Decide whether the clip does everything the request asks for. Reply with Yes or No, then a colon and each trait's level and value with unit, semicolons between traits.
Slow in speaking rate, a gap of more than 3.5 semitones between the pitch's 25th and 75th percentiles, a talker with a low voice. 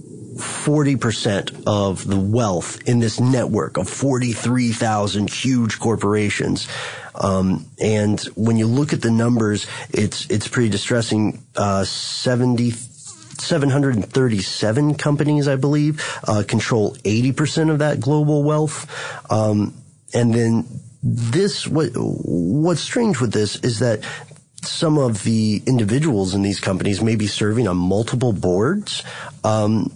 Yes: slow, 130 wpm; average, 4.7 semitones; low, 120 Hz